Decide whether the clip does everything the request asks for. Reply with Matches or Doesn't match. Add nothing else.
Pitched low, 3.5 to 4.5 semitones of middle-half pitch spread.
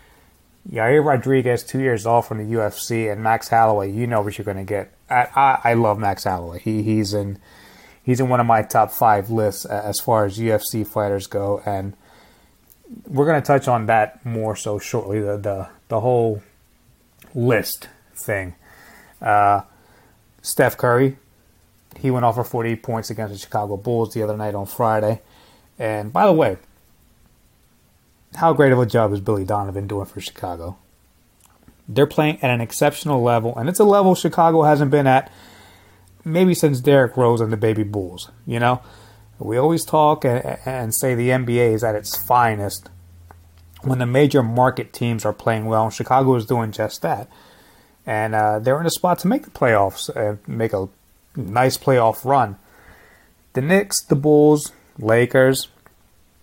Matches